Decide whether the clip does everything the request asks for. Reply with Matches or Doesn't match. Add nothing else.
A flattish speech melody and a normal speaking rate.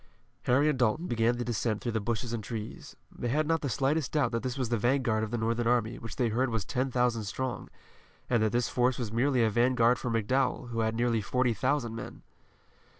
Doesn't match